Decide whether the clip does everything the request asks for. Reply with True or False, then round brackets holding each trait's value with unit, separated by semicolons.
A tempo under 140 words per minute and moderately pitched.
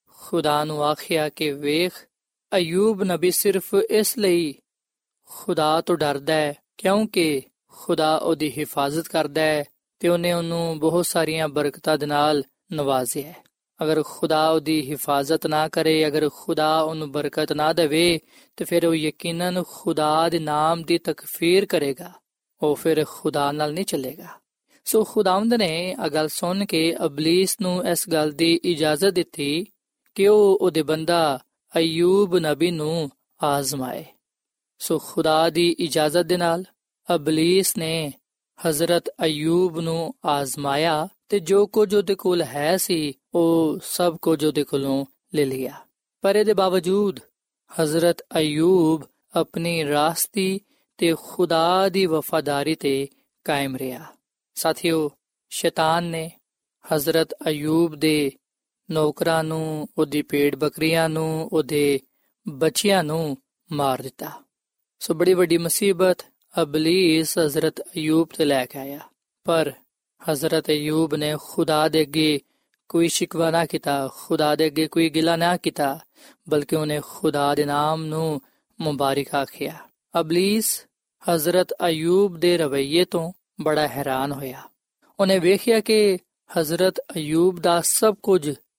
True (130 wpm; 160 Hz)